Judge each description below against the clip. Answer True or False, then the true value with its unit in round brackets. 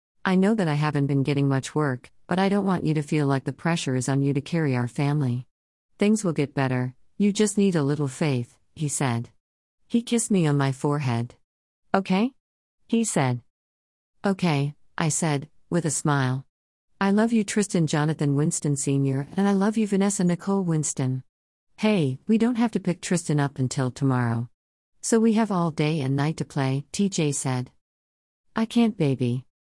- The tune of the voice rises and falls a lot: True (6.4 semitones)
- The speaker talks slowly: False (185 wpm)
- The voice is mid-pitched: True (145 Hz)